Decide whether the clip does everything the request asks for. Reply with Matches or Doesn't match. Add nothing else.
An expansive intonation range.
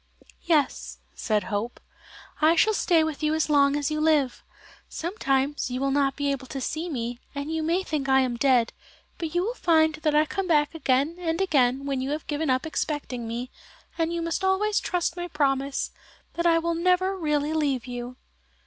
Doesn't match